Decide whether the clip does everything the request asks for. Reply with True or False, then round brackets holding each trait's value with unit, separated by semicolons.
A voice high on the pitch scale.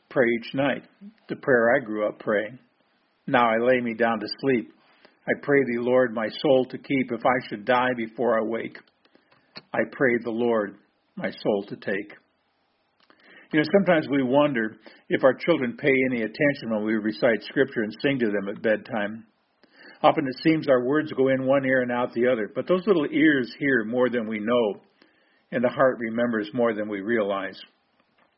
False (120 Hz)